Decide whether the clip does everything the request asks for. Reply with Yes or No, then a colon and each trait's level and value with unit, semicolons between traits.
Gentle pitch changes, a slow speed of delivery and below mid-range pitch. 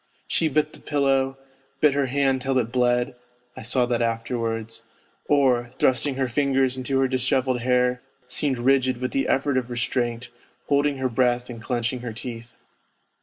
No: narrow, 1.9 semitones; average, 165 wpm; low, 125 Hz